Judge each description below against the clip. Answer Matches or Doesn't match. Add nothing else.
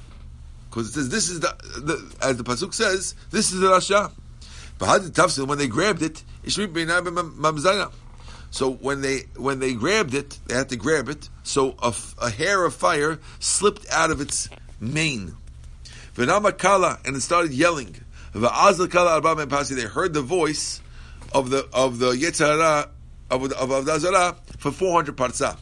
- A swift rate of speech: Doesn't match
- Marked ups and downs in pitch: Matches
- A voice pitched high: Doesn't match